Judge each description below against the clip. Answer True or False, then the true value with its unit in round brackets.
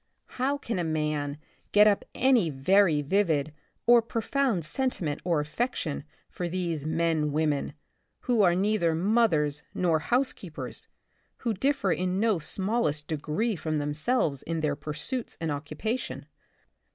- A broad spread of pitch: True (6.4 semitones)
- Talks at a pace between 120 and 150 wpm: True (135 wpm)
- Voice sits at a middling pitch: True (170 Hz)